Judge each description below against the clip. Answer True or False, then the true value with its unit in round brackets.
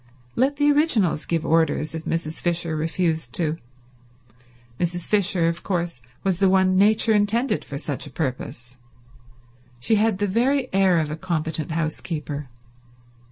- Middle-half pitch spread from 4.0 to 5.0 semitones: True (4.5 semitones)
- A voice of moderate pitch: True (170 Hz)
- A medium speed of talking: True (145 wpm)